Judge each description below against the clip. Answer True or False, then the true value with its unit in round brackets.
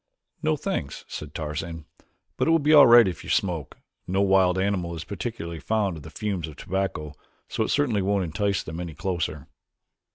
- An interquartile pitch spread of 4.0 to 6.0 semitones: True (4.3 semitones)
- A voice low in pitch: True (95 Hz)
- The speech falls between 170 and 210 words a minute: True (190 wpm)